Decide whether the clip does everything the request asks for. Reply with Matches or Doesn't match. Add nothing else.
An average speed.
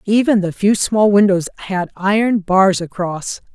Matches